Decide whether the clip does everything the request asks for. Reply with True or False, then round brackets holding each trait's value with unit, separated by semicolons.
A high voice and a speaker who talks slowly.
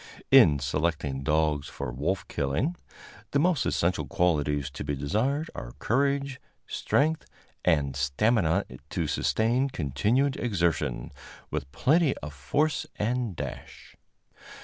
False (90 Hz; 115 wpm)